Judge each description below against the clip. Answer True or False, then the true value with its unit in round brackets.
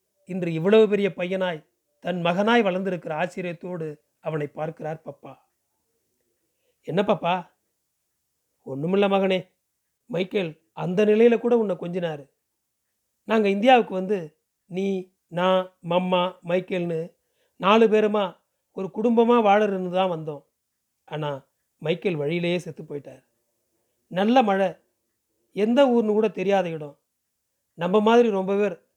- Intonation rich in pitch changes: False (4.1 semitones)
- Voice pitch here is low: False (185 Hz)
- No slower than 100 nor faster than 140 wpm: True (105 wpm)